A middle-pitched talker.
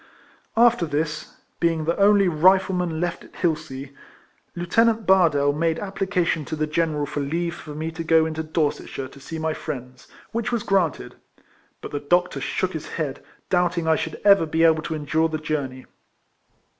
Yes: medium, 160 Hz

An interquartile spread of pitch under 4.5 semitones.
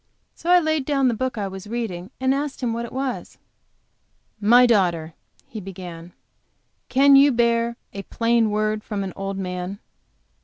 No: average, 4.9 semitones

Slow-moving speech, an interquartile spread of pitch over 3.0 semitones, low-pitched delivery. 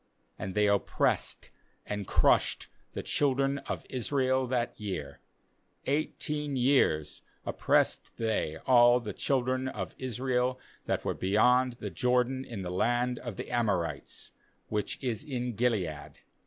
Yes: slow, 130 wpm; average, 3.9 semitones; low, 125 Hz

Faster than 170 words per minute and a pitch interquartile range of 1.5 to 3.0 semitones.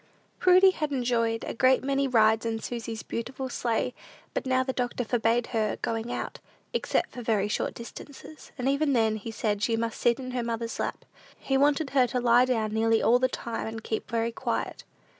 Yes: average, 195 wpm; narrow, 2.4 semitones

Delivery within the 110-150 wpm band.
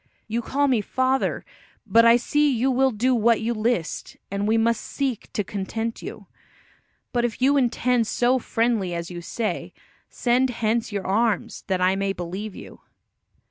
No: average, 170 wpm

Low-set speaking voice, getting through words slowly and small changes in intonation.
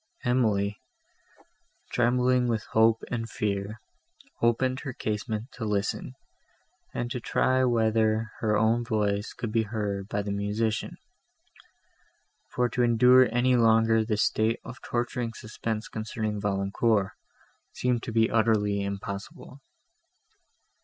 Yes: low, 110 Hz; slow, 120 wpm; narrow, 2.3 semitones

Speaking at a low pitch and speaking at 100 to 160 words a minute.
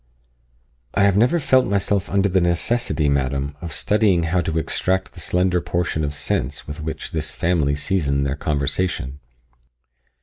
Yes: very low, 85 Hz; average, 155 wpm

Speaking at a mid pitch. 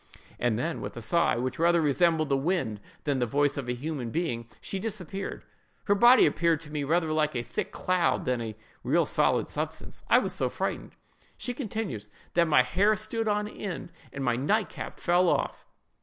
Yes: medium, 160 Hz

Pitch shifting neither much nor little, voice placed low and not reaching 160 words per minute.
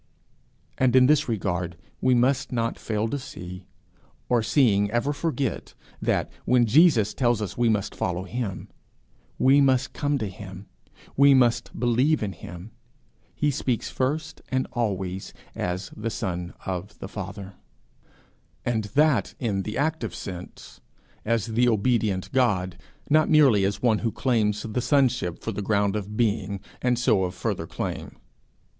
Yes: average, 4.6 semitones; low, 115 Hz; average, 150 wpm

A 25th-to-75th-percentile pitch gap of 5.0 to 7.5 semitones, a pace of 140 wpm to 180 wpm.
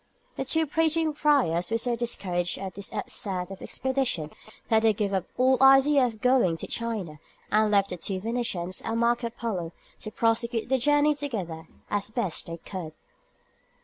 Yes: wide, 5.6 semitones; average, 175 wpm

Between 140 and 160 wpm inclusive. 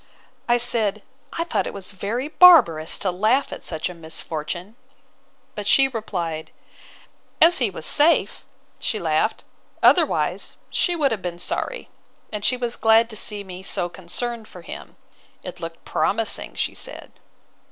Yes: average, 150 wpm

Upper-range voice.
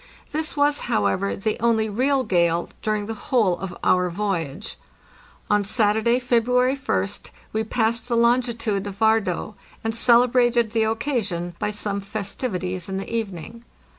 Yes: high, 220 Hz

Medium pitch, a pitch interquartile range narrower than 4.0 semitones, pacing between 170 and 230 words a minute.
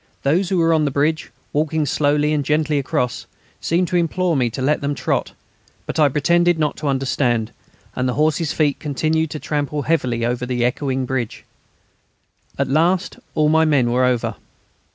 Yes: medium, 150 Hz; average, 3.4 semitones; average, 175 wpm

